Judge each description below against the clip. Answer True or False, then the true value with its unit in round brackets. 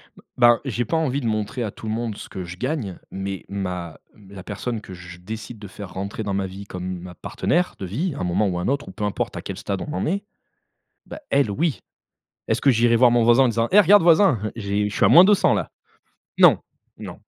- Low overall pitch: True (110 Hz)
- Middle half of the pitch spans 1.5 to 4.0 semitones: False (5.1 semitones)